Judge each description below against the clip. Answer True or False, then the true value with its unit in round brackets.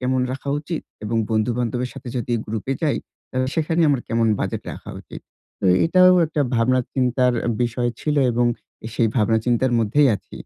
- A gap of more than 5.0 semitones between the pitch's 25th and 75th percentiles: False (3.3 semitones)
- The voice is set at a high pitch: False (125 Hz)